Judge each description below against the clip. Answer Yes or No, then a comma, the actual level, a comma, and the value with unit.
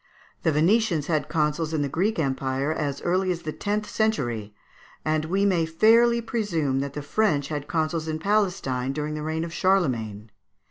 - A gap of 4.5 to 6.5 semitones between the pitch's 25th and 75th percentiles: Yes, average, 5.1 semitones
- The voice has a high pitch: No, medium, 160 Hz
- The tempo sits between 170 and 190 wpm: Yes, average, 175 wpm